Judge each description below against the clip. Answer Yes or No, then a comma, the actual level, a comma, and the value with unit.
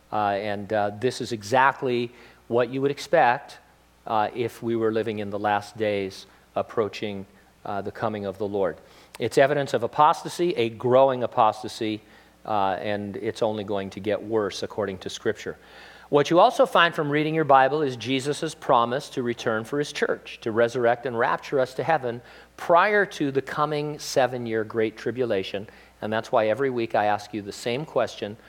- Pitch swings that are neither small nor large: Yes, average, 4.7 semitones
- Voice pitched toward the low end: Yes, low, 115 Hz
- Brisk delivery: No, average, 180 wpm